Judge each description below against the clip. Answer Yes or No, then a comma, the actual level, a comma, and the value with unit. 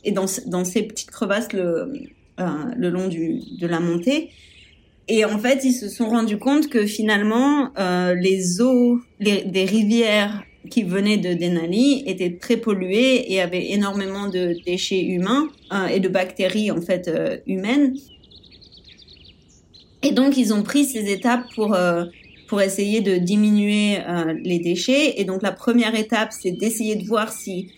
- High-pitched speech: Yes, high, 205 Hz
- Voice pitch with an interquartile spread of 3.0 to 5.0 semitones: Yes, average, 4.0 semitones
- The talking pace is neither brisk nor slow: Yes, average, 165 wpm